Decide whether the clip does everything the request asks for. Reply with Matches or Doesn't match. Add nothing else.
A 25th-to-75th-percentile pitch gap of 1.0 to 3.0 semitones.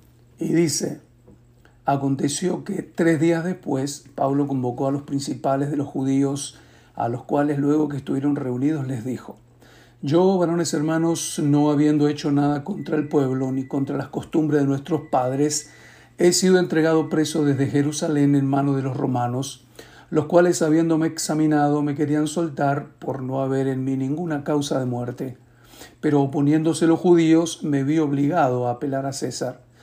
Matches